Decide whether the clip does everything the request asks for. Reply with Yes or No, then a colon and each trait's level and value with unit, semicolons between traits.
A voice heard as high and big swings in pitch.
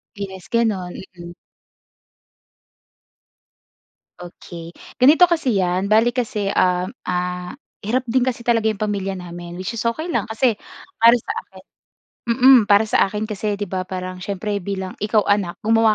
No: high, 205 Hz; average, 4.0 semitones